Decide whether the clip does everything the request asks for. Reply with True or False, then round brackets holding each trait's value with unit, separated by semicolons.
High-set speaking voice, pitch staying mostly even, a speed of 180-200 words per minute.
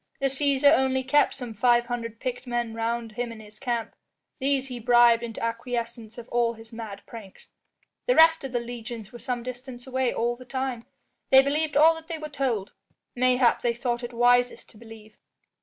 True (240 Hz; 2.3 semitones; 190 wpm)